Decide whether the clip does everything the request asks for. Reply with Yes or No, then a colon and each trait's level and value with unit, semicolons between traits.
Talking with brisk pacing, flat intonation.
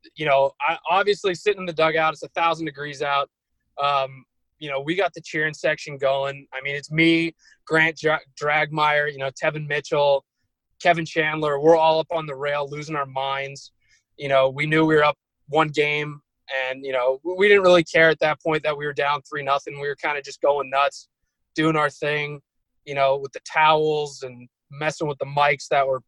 Yes: fast, 210 wpm; narrow, 2.2 semitones